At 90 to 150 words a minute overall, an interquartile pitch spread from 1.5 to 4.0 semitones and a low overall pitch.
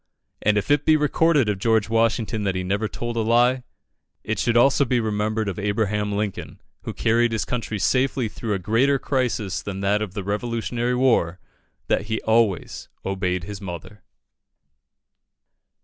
No: average, 165 wpm; average, 2.8 semitones; low, 110 Hz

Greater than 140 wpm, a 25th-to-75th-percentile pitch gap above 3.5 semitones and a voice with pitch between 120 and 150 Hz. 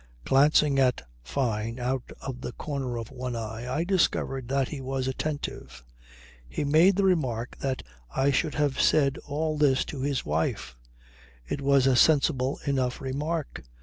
No: average, 155 wpm; average, 2.7 semitones; low, 135 Hz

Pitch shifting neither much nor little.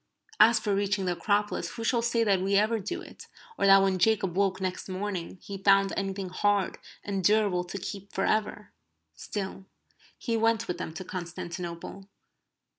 No: narrow, 1.9 semitones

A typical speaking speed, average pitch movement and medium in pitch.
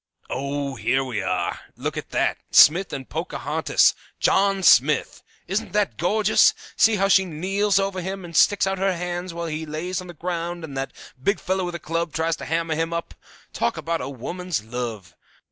Yes: average, 185 wpm; average, 3.8 semitones; medium, 170 Hz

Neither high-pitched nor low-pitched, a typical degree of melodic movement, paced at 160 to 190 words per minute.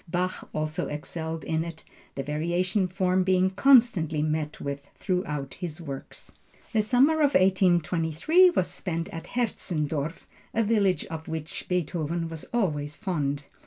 No: medium, 170 Hz; average, 3.5 semitones; slow, 135 wpm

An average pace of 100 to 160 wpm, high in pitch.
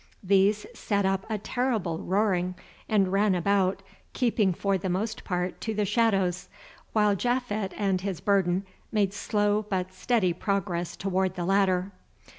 Yes: average, 145 wpm; high, 195 Hz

